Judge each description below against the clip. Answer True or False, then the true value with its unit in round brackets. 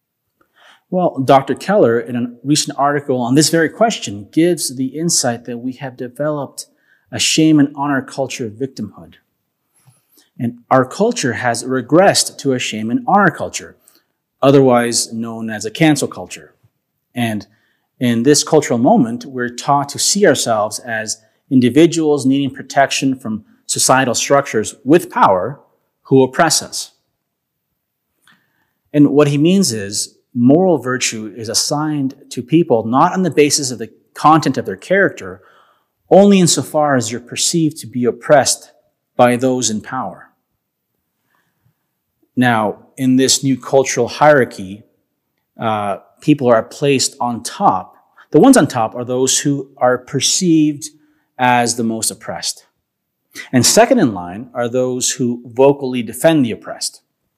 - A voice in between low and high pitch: False (130 Hz)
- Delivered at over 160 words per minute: False (140 wpm)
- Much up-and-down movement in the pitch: False (3.6 semitones)